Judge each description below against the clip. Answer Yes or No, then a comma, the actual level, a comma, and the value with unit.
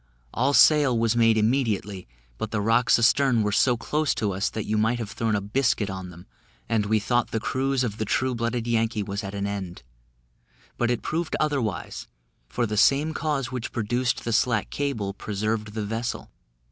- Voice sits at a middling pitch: No, low, 115 Hz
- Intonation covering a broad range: No, average, 3.2 semitones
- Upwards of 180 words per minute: Yes, average, 190 wpm